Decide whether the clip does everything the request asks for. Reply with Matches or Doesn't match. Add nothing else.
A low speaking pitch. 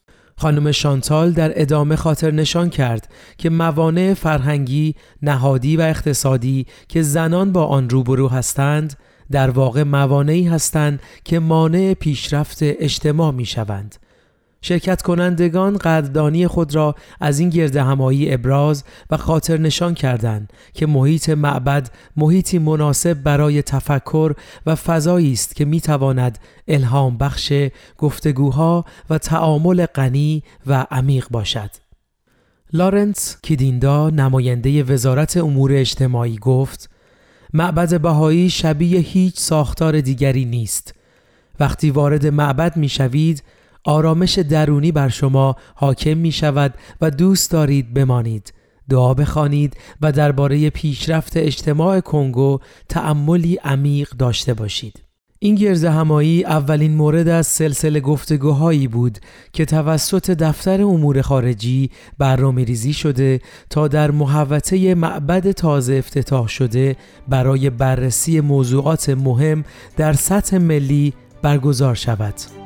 Doesn't match